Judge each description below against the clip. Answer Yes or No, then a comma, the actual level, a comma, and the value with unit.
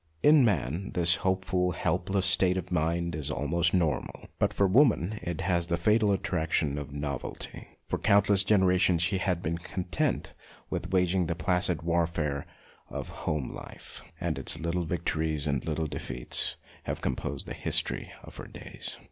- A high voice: No, very low, 85 Hz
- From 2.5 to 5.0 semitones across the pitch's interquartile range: Yes, average, 3.0 semitones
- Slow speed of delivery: No, average, 165 wpm